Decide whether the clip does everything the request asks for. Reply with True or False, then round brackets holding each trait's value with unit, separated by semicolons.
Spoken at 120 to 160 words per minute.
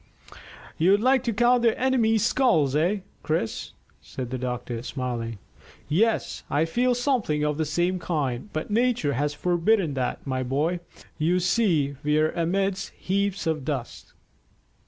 True (145 wpm)